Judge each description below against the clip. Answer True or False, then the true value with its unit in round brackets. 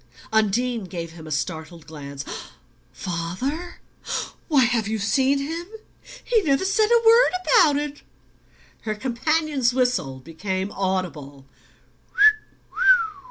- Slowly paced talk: True (110 wpm)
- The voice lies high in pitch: True (225 Hz)